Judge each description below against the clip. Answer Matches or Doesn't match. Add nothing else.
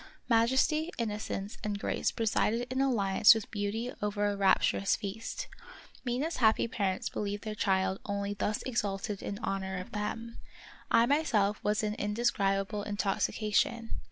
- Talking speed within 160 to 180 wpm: Doesn't match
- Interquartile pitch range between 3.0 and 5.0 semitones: Doesn't match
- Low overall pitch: Doesn't match